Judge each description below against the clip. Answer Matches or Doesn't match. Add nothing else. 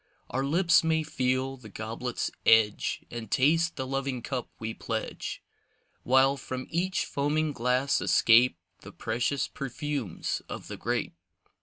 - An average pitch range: Matches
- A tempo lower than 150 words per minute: Matches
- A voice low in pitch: Matches